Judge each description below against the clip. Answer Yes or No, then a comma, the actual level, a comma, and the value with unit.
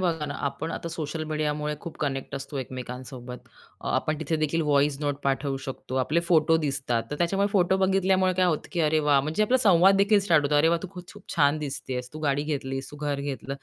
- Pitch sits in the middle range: Yes, medium, 150 Hz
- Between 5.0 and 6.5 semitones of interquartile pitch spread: No, average, 3.6 semitones